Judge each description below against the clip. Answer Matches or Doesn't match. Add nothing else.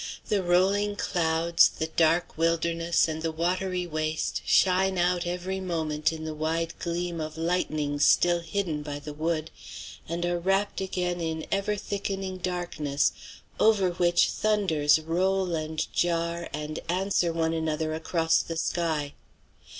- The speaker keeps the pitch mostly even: Matches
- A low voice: Doesn't match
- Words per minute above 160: Doesn't match